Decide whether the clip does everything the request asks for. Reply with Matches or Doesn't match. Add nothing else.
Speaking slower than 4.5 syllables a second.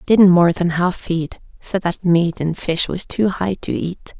Matches